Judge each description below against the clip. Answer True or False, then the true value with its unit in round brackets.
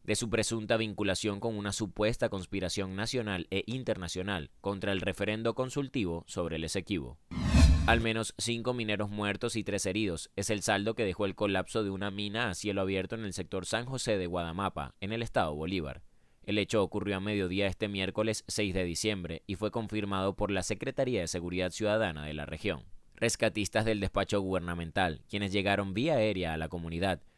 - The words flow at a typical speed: True (180 wpm)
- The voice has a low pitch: True (100 Hz)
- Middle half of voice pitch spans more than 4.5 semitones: False (2.8 semitones)